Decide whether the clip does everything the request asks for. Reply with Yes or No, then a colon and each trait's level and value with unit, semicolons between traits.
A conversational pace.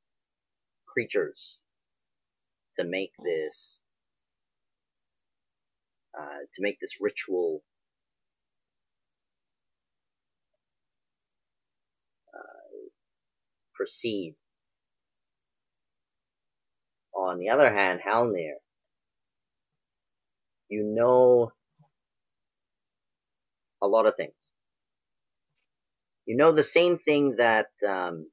No: slow, 60 wpm